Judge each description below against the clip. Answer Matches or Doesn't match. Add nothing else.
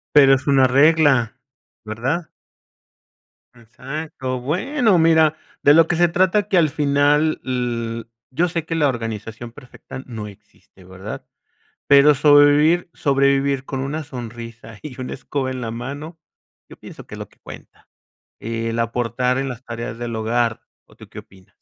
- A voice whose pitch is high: Doesn't match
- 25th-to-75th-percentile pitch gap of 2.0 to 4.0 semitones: Doesn't match